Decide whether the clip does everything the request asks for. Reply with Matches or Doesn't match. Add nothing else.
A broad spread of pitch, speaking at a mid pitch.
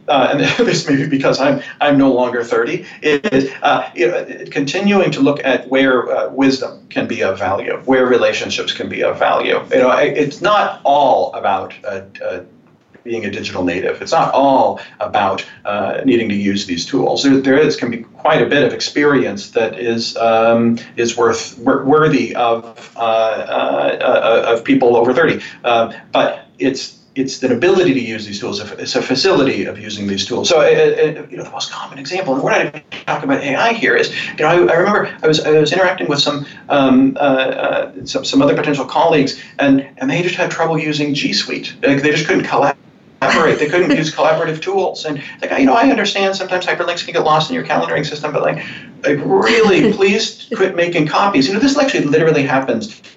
Matches